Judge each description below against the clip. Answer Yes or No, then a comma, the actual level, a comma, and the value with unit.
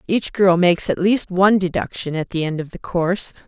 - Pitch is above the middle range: No, medium, 180 Hz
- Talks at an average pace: No, fast, 225 wpm